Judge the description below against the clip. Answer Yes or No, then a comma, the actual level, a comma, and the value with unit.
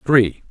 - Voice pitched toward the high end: No, low, 120 Hz